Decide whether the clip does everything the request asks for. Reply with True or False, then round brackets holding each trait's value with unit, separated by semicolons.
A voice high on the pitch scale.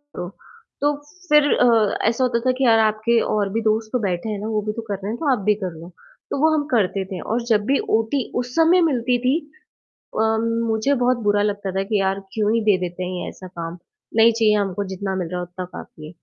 True (215 Hz)